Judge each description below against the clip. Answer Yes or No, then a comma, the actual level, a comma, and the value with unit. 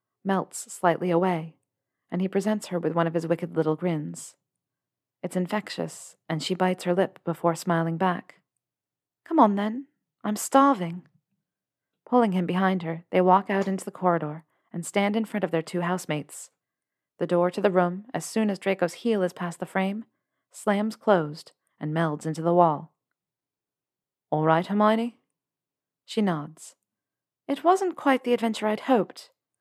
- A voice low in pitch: No, medium, 185 Hz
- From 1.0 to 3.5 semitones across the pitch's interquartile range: No, average, 3.9 semitones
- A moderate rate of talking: Yes, average, 160 wpm